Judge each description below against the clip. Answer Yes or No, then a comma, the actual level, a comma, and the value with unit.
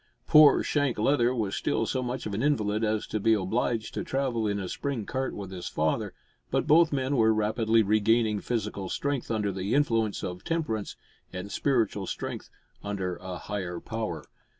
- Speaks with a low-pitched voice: Yes, low, 110 Hz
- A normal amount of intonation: Yes, average, 3.8 semitones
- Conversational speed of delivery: Yes, average, 175 wpm